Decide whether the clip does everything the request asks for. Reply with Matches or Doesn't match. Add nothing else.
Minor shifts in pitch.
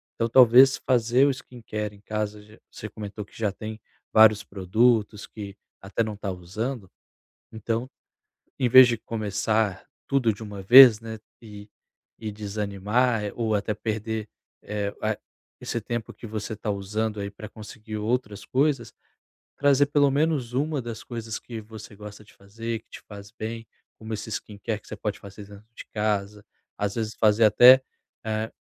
Matches